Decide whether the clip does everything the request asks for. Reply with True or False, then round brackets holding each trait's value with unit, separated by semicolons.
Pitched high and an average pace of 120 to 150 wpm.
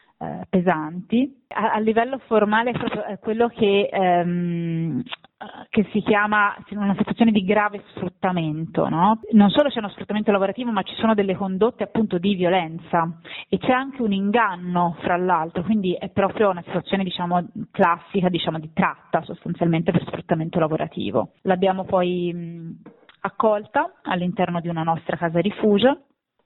True (195 Hz; 145 wpm)